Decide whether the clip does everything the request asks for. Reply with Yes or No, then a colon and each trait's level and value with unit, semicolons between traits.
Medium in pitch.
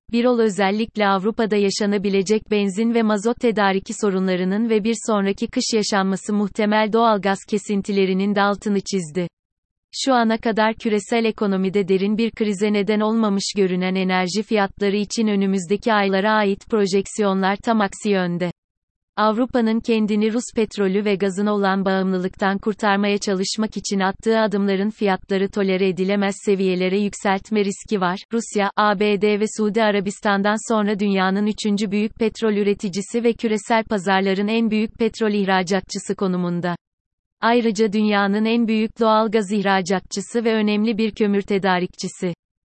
No: high, 205 Hz